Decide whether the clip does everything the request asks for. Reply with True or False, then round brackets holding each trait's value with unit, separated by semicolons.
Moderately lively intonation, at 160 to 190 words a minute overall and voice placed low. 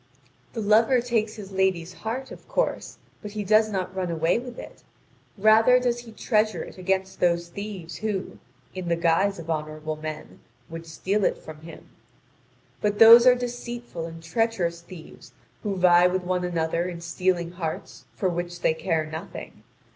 False (4.4 semitones; 170 wpm; 185 Hz)